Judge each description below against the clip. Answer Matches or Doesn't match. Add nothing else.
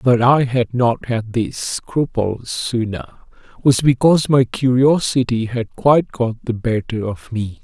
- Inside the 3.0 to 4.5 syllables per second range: Matches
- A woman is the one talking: Doesn't match